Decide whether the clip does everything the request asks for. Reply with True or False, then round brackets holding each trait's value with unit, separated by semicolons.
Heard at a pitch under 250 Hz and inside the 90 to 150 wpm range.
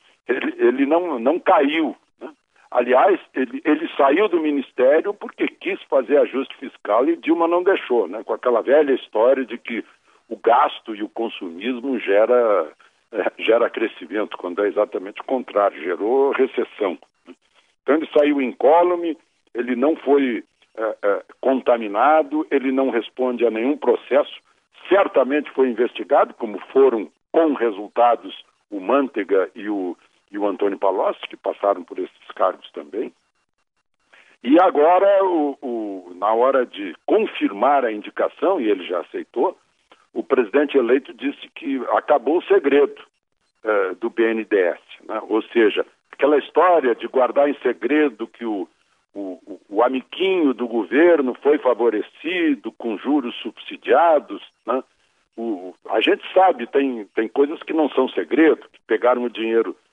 True (185 Hz; 145 wpm)